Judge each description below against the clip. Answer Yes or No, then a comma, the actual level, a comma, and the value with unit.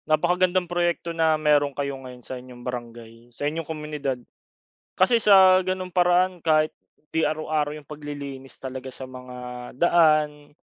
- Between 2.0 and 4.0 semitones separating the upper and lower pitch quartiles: No, average, 4.5 semitones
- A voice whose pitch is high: No, medium, 150 Hz